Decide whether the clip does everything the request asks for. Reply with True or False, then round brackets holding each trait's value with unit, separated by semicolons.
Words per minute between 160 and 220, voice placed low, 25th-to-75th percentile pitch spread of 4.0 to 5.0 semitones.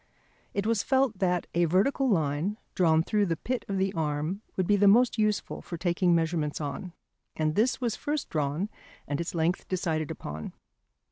False (180 wpm; 180 Hz; 4.7 semitones)